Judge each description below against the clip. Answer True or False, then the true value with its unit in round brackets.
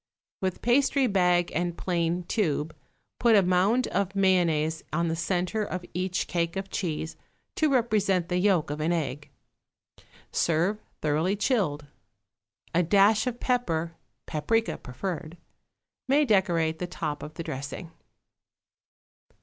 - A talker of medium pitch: True (180 Hz)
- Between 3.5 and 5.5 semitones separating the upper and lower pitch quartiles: True (3.8 semitones)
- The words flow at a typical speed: False (130 wpm)